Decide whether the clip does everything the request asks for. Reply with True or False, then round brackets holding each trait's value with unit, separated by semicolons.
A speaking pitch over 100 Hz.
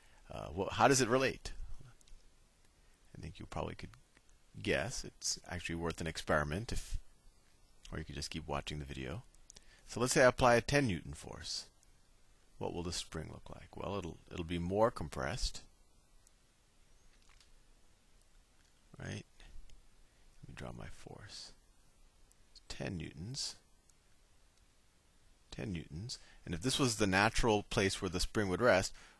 False (90 Hz)